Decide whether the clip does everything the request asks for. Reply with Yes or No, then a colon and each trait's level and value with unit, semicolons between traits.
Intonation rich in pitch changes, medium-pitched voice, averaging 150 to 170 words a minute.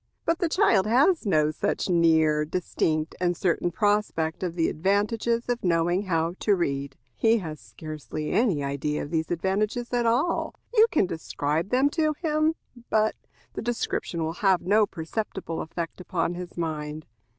Yes: wide, 5.7 semitones; medium, 180 Hz; average, 160 wpm